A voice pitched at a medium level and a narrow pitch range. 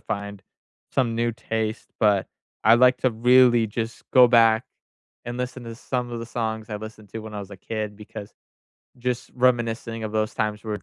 No: low, 115 Hz; narrow, 2.0 semitones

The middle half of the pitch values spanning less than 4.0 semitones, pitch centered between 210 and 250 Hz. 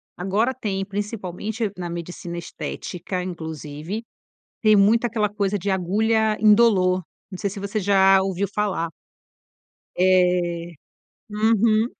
No: average, 3.0 semitones; high, 195 Hz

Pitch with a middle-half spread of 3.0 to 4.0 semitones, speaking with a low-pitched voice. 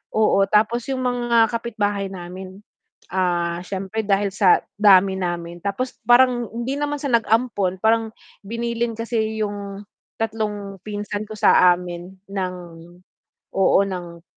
No: average, 3.3 semitones; high, 205 Hz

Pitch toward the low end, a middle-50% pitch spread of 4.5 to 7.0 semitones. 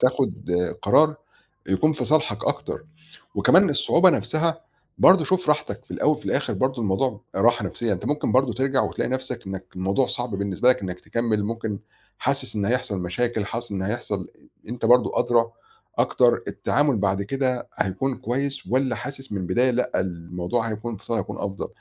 Yes: low, 120 Hz; average, 4.9 semitones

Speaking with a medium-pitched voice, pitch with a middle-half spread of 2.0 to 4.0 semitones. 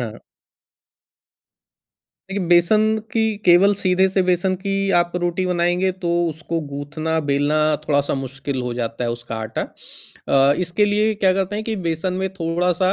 No: medium, 175 Hz; average, 5.0 semitones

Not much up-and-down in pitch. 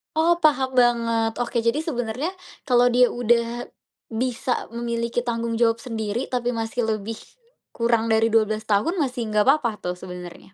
Yes: narrow, 1.7 semitones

